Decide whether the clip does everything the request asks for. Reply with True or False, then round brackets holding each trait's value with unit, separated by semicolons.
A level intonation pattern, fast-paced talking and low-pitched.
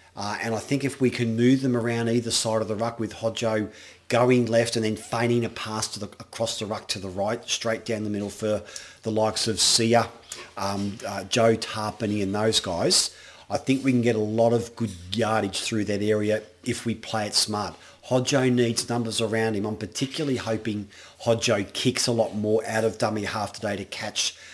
True (1.8 semitones; 210 wpm; 110 Hz)